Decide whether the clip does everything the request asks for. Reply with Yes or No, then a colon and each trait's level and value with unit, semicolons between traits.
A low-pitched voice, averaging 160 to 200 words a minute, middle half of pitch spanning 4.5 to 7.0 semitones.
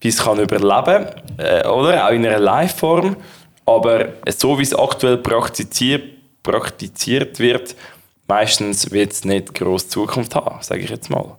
No: low, 115 Hz; average, 150 wpm; average, 4.8 semitones